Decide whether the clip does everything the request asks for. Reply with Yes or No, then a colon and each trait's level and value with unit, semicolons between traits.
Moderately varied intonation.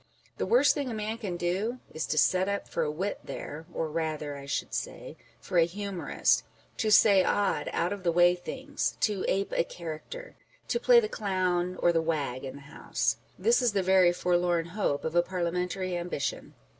Yes: average, 3.5 semitones